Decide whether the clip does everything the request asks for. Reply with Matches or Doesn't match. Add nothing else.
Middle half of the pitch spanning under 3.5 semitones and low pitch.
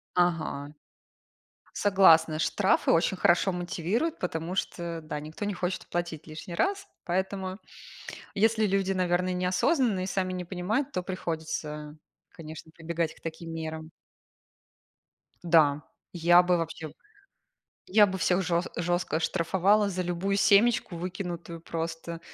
Doesn't match